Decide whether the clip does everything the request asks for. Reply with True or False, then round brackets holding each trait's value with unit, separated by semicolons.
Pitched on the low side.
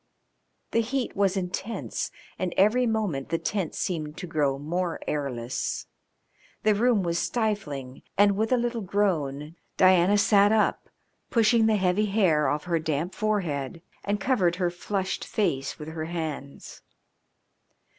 False (185 Hz)